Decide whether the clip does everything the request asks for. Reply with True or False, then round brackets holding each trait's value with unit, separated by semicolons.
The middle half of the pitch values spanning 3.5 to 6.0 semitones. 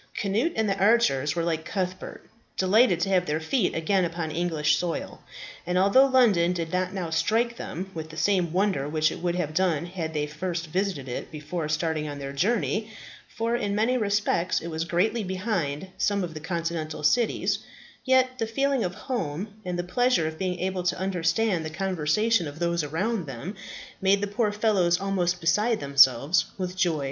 True (4.2 semitones)